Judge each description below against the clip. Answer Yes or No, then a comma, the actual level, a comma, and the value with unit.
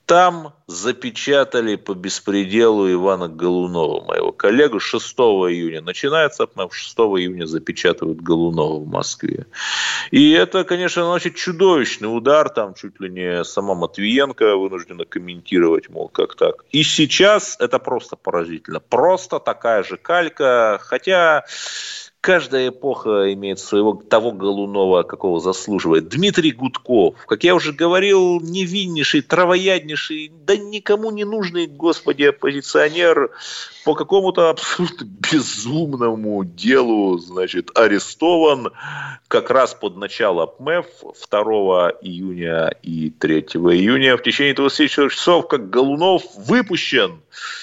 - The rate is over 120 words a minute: No, average, 115 wpm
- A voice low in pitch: No, medium, 150 Hz